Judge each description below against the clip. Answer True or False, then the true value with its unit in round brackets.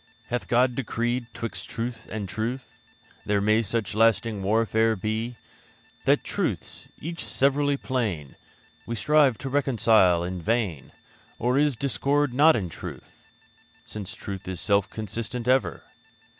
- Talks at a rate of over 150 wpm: False (135 wpm)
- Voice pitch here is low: True (115 Hz)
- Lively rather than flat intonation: False (3.7 semitones)